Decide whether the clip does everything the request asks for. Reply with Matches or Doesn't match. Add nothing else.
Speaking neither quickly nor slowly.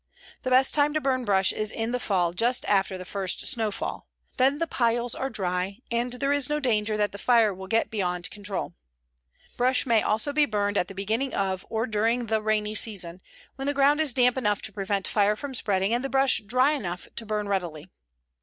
Doesn't match